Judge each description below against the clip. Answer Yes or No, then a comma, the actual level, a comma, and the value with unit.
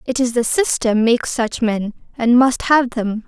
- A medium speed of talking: Yes, average, 185 wpm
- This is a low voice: No, high, 240 Hz